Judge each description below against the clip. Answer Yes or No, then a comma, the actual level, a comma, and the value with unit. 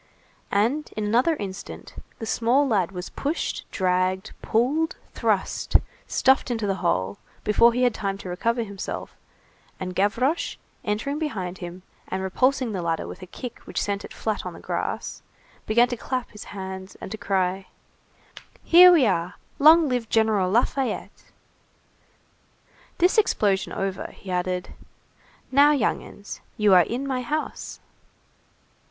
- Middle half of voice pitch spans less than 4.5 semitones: No, average, 5.3 semitones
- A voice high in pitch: Yes, high, 215 Hz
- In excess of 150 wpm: No, average, 145 wpm